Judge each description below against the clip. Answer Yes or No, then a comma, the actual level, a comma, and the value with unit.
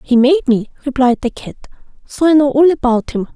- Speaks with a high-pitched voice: Yes, very high, 270 Hz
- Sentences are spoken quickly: Yes, fast, 215 wpm